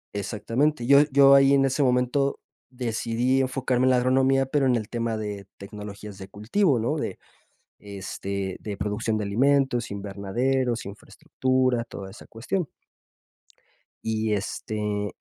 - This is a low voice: Yes, low, 120 Hz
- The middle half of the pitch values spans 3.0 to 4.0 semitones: No, average, 4.4 semitones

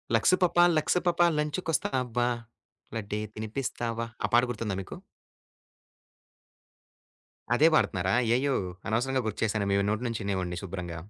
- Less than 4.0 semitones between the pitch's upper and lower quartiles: No, average, 4.7 semitones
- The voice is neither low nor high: No, low, 115 Hz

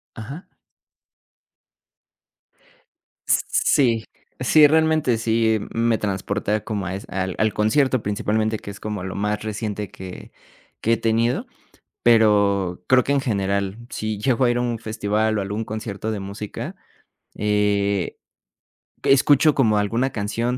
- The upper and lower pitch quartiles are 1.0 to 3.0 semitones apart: Yes, narrow, 2.5 semitones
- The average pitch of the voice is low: Yes, low, 110 Hz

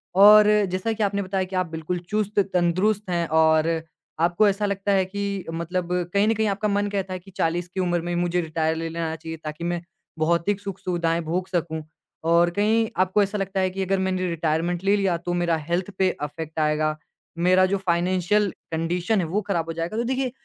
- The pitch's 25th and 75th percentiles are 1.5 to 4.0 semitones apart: Yes, average, 2.8 semitones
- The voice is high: No, medium, 180 Hz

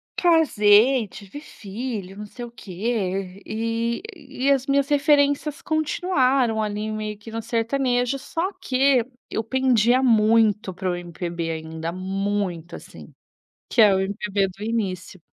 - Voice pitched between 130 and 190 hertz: No, high, 225 Hz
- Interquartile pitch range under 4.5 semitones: No, average, 5.1 semitones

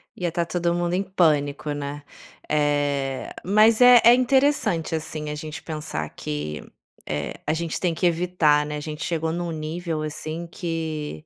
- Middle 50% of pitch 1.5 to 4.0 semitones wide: Yes, average, 2.8 semitones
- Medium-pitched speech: Yes, medium, 160 Hz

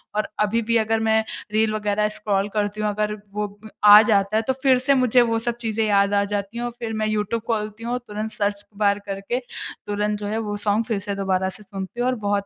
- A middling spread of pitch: No, narrow, 1.6 semitones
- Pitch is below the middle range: No, high, 210 Hz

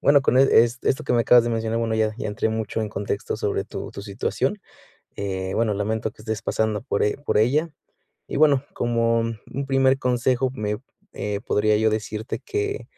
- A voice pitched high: No, low, 115 Hz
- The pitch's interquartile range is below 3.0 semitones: No, average, 3.5 semitones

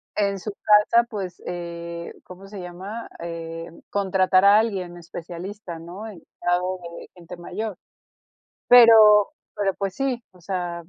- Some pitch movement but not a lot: Yes, average, 3.2 semitones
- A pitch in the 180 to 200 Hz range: Yes, medium, 185 Hz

